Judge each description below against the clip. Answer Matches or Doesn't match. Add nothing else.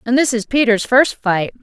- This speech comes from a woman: Matches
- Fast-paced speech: Matches